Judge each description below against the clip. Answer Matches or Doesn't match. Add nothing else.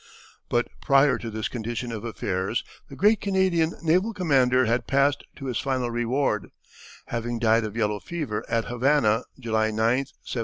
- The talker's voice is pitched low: Matches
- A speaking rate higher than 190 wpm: Doesn't match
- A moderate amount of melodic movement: Matches